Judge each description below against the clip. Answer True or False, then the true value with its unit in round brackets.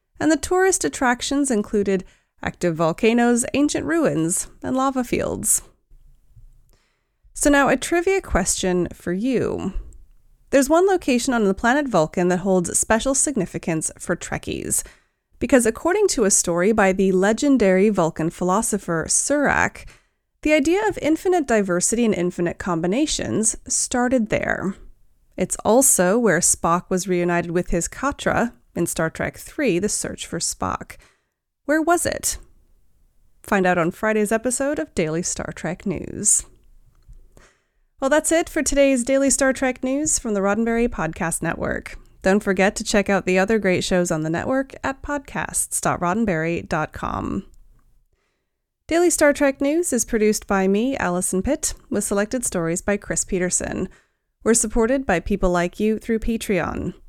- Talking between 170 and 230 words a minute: False (140 wpm)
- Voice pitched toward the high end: True (220 Hz)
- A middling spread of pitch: False (7.0 semitones)